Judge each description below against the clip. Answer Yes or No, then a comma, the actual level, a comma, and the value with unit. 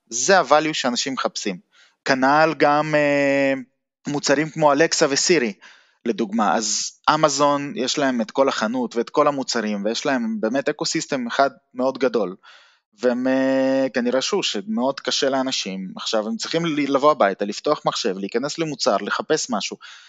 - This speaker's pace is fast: No, average, 140 wpm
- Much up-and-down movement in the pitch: No, average, 2.8 semitones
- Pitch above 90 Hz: Yes, medium, 140 Hz